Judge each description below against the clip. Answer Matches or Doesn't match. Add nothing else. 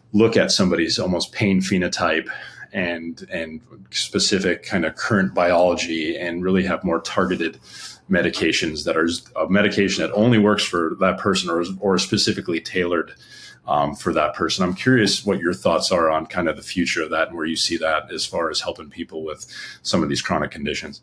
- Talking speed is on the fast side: Doesn't match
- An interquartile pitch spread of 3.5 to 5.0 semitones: Matches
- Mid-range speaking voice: Doesn't match